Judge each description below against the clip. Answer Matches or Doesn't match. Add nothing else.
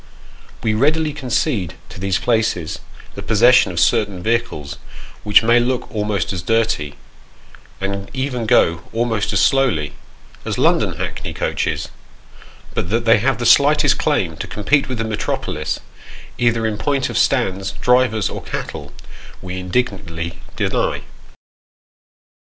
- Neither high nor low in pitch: Doesn't match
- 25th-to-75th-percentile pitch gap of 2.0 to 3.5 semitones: Doesn't match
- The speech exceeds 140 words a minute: Doesn't match